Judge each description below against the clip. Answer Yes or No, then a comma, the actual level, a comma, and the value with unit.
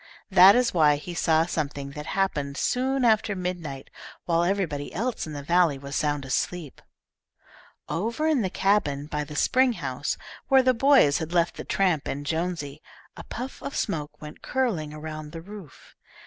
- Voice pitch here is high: No, medium, 165 Hz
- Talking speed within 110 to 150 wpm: No, average, 170 wpm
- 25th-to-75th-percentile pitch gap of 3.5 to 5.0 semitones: No, wide, 5.5 semitones